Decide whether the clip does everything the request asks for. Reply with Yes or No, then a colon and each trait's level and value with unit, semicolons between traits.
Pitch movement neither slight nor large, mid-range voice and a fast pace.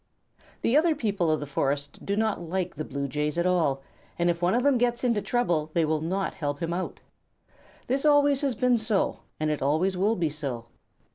No: wide, 7.5 semitones; medium, 175 Hz; fast, 210 wpm